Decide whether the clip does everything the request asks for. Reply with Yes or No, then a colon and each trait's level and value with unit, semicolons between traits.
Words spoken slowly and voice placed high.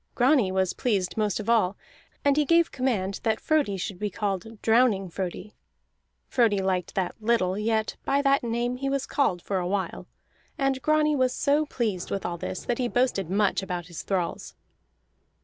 No: average, 180 wpm; high, 215 Hz